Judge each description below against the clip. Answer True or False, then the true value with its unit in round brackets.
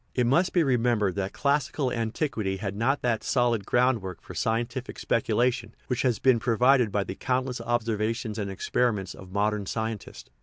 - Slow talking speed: False (165 wpm)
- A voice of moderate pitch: False (115 Hz)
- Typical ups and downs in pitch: True (3.1 semitones)